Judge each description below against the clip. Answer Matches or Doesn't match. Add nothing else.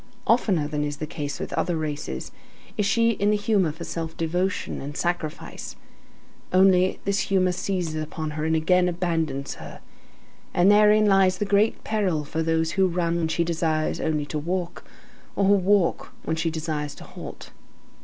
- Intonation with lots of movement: Doesn't match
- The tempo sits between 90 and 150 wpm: Doesn't match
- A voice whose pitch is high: Doesn't match